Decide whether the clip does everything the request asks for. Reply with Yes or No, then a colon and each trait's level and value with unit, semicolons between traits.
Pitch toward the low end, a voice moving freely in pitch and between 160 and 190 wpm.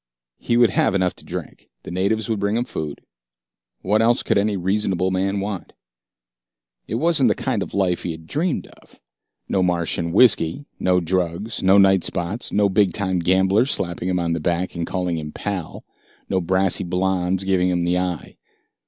No: very low, 95 Hz; narrow, 2.5 semitones; average, 180 wpm